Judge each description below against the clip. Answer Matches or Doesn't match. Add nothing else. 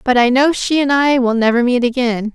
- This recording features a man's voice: Doesn't match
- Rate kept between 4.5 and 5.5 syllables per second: Matches